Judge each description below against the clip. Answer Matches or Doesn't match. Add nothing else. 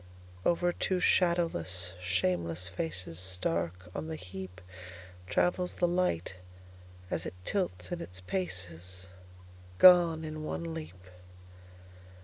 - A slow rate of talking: Matches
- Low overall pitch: Matches